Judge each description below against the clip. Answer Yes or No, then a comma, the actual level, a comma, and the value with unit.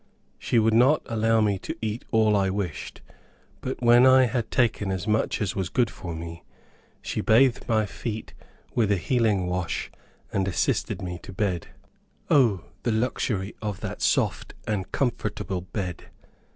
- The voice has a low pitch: Yes, low, 105 Hz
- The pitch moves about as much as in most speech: Yes, average, 3.6 semitones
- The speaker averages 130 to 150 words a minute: No, average, 160 wpm